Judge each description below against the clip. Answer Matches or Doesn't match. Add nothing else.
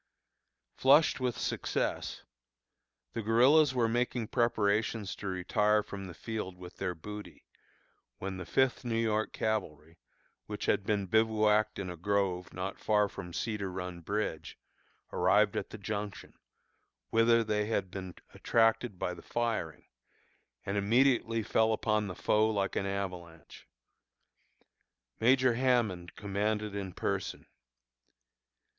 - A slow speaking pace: Matches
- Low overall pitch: Matches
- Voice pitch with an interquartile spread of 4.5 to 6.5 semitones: Doesn't match